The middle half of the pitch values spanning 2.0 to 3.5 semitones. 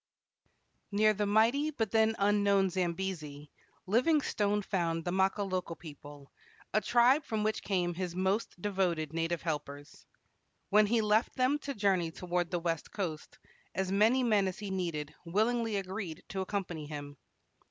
No: average, 4.0 semitones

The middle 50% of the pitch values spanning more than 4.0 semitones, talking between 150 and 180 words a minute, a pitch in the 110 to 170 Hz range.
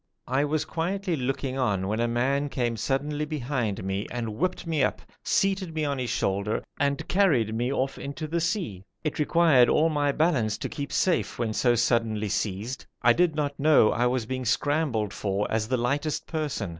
No: average, 5.0 semitones; average, 190 wpm; low, 135 Hz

